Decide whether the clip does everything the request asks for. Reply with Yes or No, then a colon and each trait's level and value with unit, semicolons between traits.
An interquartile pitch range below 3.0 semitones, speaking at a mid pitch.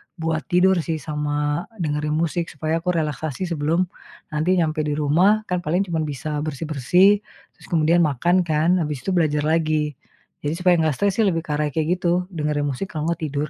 Yes: narrow, 2.6 semitones; medium, 160 Hz